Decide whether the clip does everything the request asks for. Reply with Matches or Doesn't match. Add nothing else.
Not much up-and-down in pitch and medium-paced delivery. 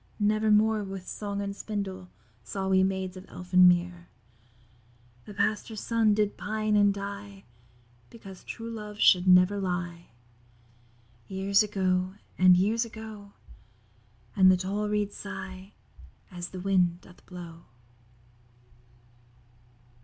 Doesn't match